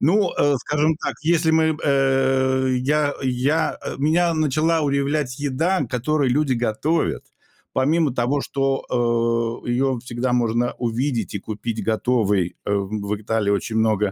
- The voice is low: Yes, low, 130 Hz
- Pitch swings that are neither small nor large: Yes, average, 4.2 semitones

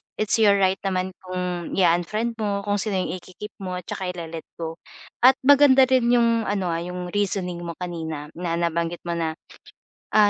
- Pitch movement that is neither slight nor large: Yes, average, 3.5 semitones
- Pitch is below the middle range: No, medium, 185 Hz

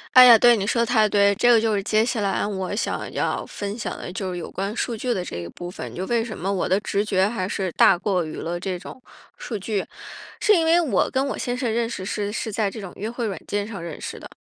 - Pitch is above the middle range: Yes, high, 205 Hz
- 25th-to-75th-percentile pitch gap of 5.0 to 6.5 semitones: No, average, 3.6 semitones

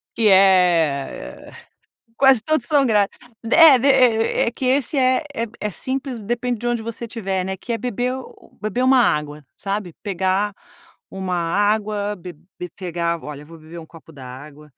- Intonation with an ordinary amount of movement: No, wide, 5.9 semitones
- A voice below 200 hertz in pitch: No, high, 205 Hz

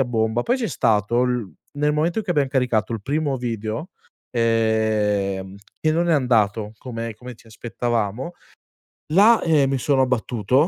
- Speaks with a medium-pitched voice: No, low, 120 Hz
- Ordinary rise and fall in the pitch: Yes, average, 4.6 semitones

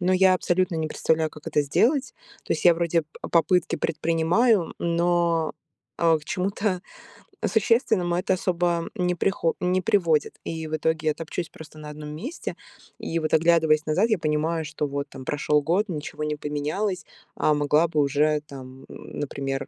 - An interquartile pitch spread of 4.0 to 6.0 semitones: No, average, 2.9 semitones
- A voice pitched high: No, medium, 165 Hz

